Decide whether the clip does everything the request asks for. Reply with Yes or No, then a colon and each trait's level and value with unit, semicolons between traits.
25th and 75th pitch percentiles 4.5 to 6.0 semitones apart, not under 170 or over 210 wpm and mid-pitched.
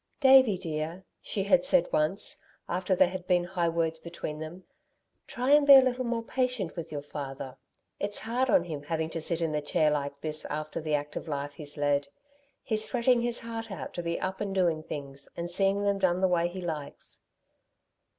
Yes: average, 5.1 semitones; average, 200 wpm; medium, 175 Hz